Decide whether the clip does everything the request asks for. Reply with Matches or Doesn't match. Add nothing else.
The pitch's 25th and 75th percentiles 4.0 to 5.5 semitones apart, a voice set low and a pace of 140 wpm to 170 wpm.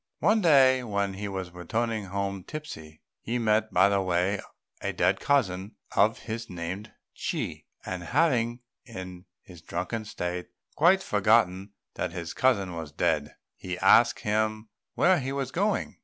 Matches